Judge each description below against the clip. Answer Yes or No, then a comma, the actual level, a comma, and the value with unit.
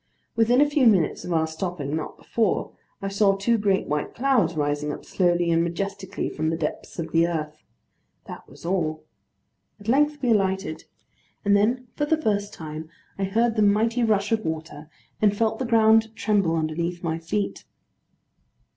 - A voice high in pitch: Yes, high, 195 Hz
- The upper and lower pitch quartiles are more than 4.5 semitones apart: Yes, average, 5.3 semitones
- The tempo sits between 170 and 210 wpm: Yes, average, 175 wpm